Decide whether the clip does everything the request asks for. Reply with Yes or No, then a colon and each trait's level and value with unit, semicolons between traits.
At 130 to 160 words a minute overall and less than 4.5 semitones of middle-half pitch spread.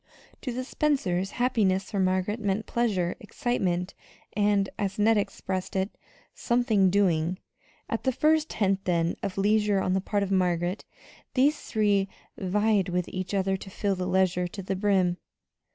Yes: average, 155 wpm; narrow, 2.5 semitones